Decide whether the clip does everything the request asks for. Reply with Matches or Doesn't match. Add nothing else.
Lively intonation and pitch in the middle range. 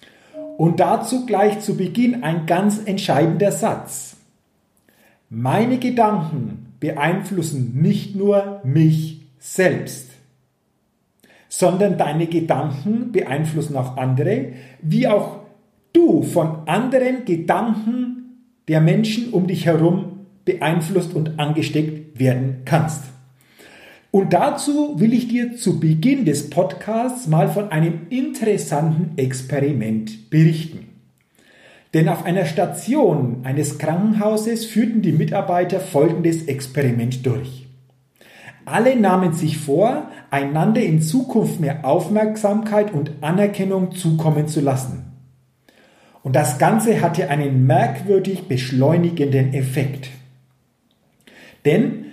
Matches